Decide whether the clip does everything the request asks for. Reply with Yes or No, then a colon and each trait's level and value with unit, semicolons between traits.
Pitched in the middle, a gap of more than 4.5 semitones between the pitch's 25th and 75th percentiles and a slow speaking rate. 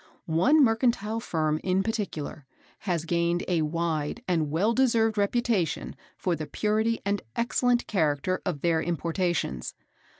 Yes: medium, 180 Hz; wide, 5.6 semitones; slow, 130 wpm